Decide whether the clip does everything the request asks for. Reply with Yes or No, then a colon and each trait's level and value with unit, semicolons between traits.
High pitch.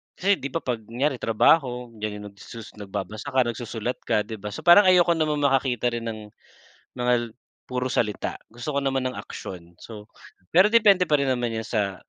No: low, 125 Hz